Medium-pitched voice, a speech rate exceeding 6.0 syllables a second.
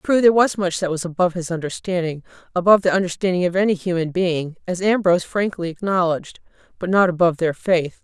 Yes: medium, 180 Hz; 6.4 syllables/s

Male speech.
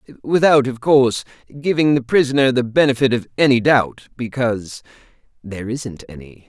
Yes: male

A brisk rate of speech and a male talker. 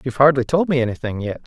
Yes: fast, 245 wpm; male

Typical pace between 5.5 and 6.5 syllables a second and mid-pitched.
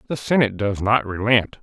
No: 5.6 syllables/s; low, 110 Hz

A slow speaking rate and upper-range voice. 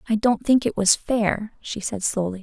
No: fast, 220 wpm; high, 215 Hz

